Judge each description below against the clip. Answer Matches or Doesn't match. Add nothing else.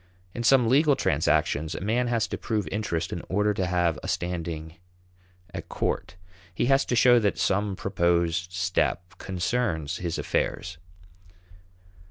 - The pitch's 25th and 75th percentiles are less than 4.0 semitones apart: Doesn't match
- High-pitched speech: Doesn't match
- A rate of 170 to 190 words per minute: Doesn't match